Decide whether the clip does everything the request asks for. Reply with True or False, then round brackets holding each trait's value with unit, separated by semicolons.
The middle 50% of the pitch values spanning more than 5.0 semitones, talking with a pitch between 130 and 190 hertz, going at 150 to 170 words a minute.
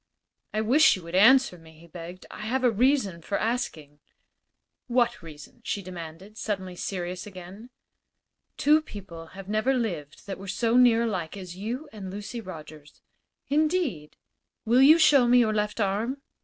False (5.4 semitones; 205 Hz; 160 wpm)